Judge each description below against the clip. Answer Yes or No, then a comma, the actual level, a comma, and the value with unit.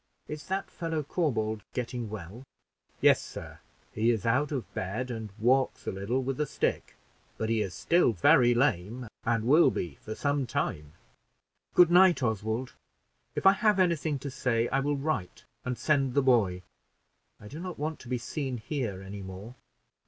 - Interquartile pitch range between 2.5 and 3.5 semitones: No, average, 5.1 semitones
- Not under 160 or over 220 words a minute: Yes, average, 175 wpm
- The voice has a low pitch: Yes, low, 125 Hz